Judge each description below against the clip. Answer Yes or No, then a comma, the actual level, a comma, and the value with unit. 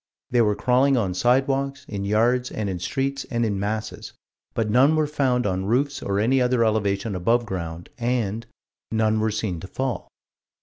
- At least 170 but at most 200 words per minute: Yes, average, 175 wpm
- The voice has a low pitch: Yes, low, 115 Hz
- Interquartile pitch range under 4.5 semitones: Yes, average, 4.0 semitones